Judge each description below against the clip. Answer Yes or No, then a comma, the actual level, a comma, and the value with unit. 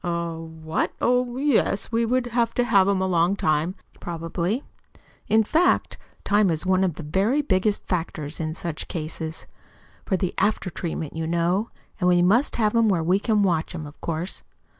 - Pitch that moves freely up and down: No, average, 4.7 semitones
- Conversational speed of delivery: Yes, average, 185 wpm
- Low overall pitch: No, medium, 185 Hz